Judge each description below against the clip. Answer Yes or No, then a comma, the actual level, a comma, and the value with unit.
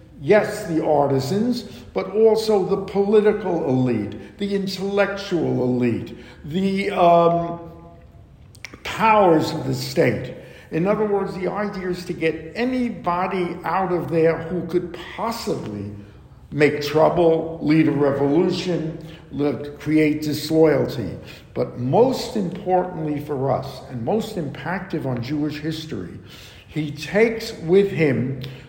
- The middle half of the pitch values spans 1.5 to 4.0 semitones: No, average, 5.1 semitones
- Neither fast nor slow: No, slow, 115 wpm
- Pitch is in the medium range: Yes, medium, 165 Hz